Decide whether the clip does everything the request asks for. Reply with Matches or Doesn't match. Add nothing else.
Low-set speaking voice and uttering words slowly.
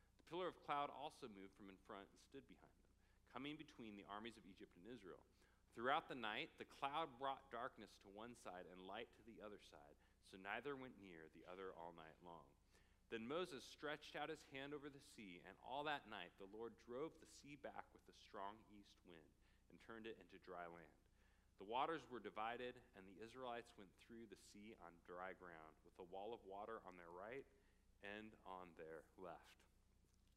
Doesn't match